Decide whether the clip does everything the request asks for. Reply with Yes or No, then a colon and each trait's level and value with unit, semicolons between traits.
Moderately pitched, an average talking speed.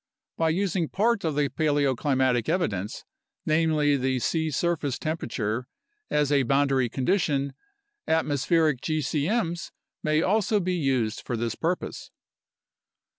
No: medium, 150 Hz; slow, 115 wpm